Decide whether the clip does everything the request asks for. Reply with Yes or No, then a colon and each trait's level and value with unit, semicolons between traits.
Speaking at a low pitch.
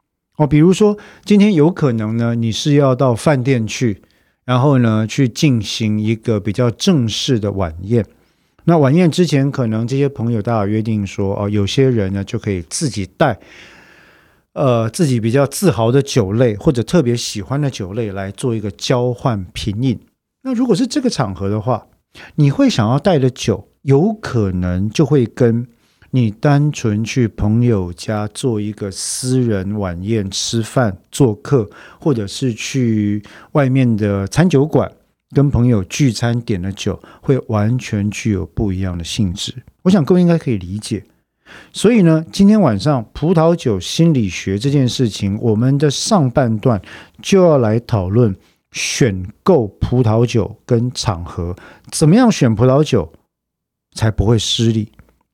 Yes: low, 120 Hz